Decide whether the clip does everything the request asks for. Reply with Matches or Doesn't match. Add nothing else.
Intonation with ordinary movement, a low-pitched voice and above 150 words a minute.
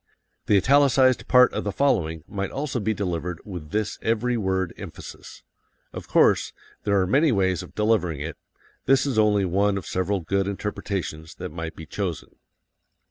Matches